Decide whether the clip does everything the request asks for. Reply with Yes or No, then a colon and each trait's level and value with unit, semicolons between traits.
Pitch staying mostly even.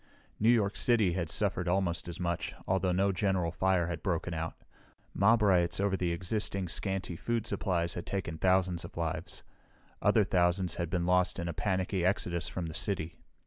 Yes: narrow, 2.2 semitones